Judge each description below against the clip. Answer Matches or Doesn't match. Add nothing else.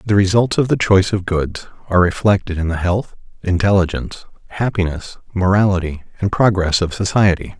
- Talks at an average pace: Matches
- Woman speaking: Doesn't match